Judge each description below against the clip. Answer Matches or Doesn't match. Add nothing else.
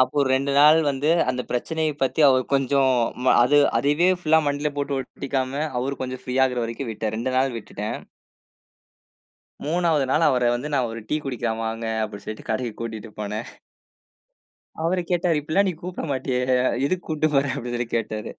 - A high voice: Doesn't match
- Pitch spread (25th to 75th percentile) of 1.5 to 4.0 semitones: Matches